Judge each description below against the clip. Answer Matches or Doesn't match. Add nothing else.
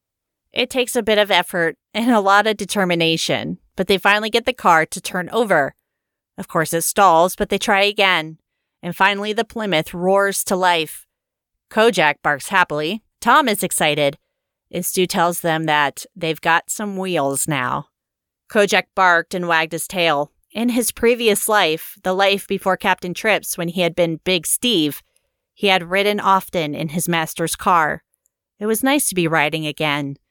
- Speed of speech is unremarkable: Matches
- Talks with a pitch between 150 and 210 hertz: Matches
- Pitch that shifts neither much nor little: Matches